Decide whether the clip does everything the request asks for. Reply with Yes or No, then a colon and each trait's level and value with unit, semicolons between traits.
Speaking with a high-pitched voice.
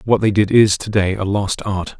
No: low, 100 Hz